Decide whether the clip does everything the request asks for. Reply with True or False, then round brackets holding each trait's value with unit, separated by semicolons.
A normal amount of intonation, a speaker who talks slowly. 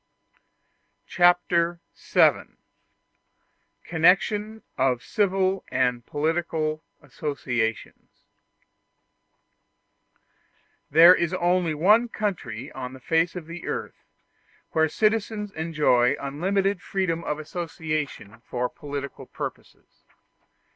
True (4.5 semitones; 85 wpm)